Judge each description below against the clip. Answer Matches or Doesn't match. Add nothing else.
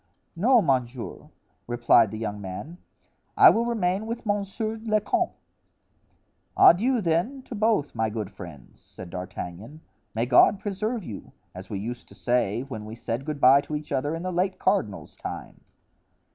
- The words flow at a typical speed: Matches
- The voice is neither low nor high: Matches